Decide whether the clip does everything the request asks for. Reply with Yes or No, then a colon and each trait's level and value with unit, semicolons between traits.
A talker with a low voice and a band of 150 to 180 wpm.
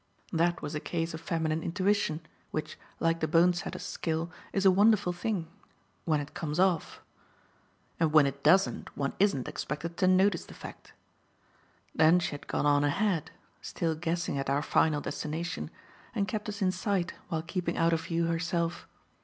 No: medium, 165 Hz; average, 170 wpm